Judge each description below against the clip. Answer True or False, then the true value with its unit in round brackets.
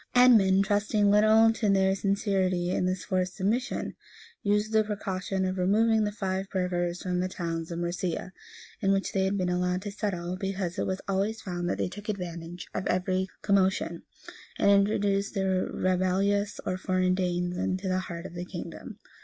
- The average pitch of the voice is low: False (190 Hz)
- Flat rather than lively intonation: True (1.9 semitones)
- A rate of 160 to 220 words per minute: True (175 wpm)